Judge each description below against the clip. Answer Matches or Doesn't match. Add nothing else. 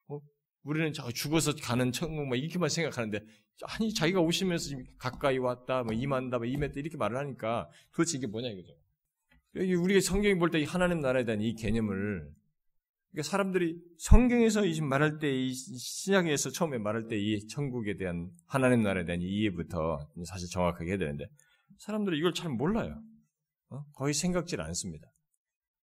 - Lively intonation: Matches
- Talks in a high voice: Doesn't match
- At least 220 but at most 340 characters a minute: Doesn't match